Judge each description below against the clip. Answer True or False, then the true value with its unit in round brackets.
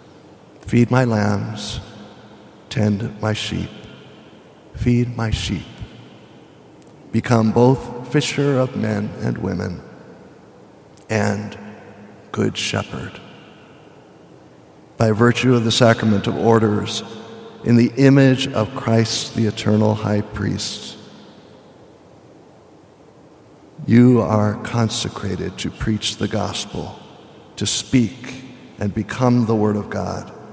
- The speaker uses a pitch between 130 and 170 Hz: False (110 Hz)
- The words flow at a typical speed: False (100 wpm)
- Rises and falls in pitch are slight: True (2.3 semitones)